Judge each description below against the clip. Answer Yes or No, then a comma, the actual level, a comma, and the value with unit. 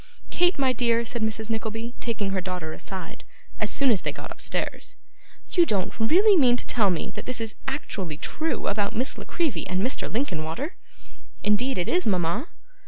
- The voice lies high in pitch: Yes, high, 225 Hz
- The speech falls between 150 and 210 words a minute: Yes, average, 180 wpm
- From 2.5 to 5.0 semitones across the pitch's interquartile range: No, wide, 5.6 semitones